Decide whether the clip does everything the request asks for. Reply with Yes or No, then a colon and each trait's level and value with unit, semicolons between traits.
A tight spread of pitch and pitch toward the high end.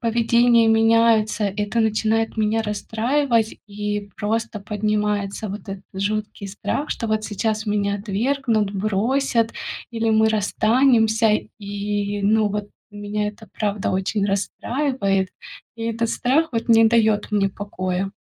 Yes: narrow, 1.9 semitones; high, 215 Hz